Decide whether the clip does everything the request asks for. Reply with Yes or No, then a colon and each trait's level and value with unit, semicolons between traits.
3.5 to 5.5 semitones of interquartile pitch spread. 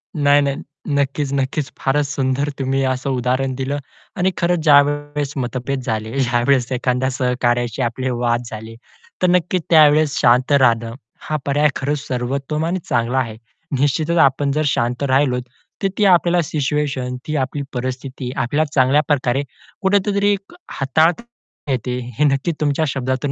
No: average, 2.7 semitones